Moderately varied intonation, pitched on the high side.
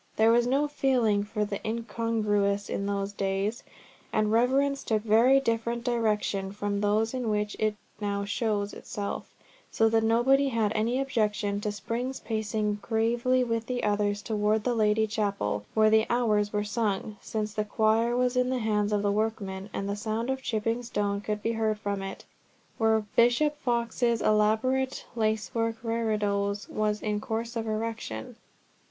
No: narrow, 2.0 semitones; high, 220 Hz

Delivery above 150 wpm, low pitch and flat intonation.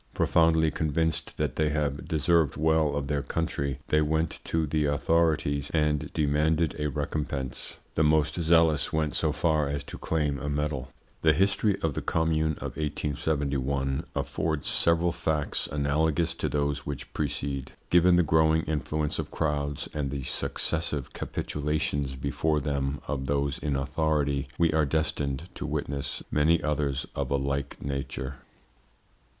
No: average, 145 wpm; very low, 75 Hz; narrow, 2.0 semitones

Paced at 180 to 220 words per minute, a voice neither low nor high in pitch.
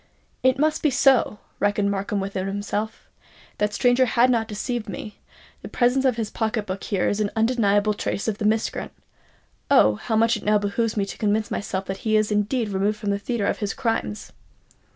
No: average, 195 wpm; high, 215 Hz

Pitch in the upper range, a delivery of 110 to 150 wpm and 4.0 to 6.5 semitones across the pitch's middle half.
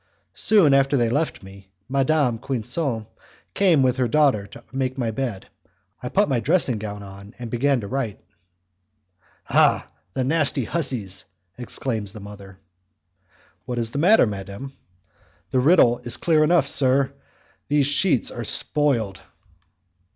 No: low, 130 Hz; average, 145 wpm; average, 4.5 semitones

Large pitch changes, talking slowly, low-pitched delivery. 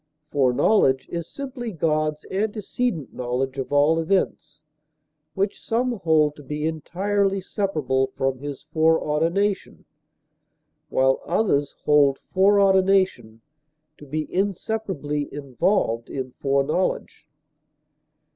No: wide, 5.9 semitones; slow, 95 wpm; medium, 155 Hz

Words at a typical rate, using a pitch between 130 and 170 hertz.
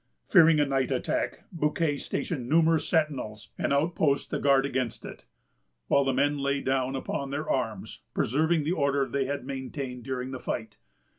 Yes: average, 165 wpm; medium, 140 Hz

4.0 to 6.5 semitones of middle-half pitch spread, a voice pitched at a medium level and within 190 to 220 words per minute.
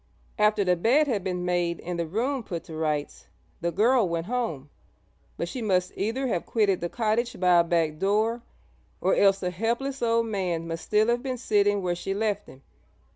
No: average, 4.9 semitones; high, 195 Hz; average, 195 wpm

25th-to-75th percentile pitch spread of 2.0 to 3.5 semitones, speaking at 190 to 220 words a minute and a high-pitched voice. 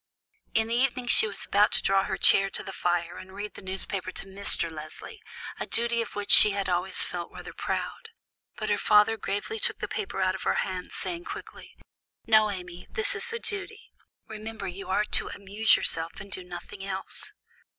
Yes: average, 3.1 semitones; average, 200 wpm; high, 200 Hz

